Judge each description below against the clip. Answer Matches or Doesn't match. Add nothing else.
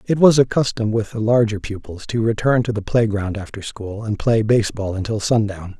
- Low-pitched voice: Matches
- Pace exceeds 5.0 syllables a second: Matches